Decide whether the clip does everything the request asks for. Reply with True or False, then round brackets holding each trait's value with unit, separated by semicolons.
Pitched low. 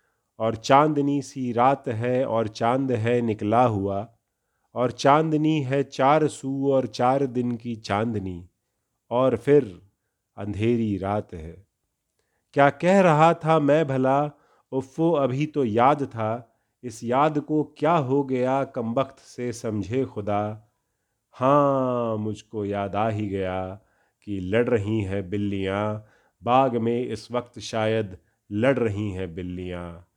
True (120 Hz)